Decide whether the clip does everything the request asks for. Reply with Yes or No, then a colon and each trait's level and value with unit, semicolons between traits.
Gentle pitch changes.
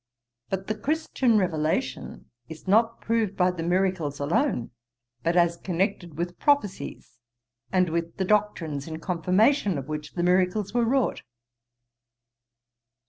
No: average, 4.2 semitones